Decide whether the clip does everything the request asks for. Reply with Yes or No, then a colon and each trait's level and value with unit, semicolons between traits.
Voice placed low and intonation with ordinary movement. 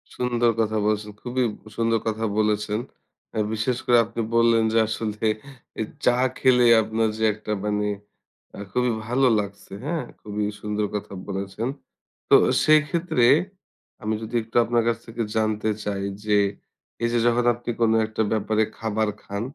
No: low, 110 Hz; narrow, 2.1 semitones